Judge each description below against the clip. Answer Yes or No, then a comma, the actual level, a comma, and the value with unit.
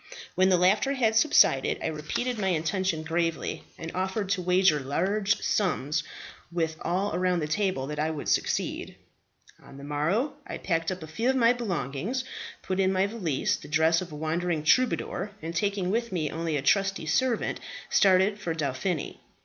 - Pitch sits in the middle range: Yes, medium, 180 Hz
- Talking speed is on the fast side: No, average, 175 wpm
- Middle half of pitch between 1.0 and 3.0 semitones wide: No, average, 4.2 semitones